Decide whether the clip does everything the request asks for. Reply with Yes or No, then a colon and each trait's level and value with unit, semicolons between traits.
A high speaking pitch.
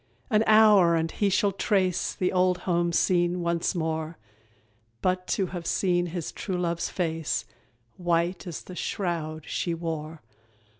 No: medium, 175 Hz